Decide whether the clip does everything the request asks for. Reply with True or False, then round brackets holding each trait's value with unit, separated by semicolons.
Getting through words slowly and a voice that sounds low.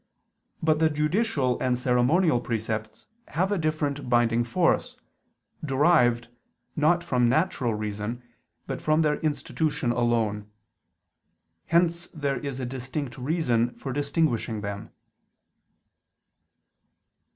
True (105 wpm; 130 Hz)